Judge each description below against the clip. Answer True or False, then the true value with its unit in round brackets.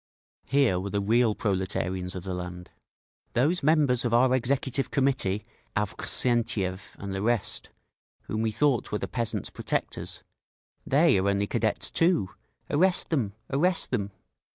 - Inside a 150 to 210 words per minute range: False (135 wpm)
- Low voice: True (115 Hz)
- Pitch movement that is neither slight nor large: False (5.7 semitones)